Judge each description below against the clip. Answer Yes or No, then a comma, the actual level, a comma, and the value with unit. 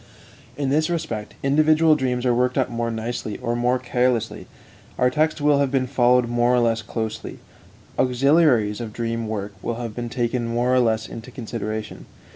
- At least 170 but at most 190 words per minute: Yes, average, 180 wpm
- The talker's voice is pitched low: Yes, low, 120 Hz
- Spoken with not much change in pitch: Yes, narrow, 2.3 semitones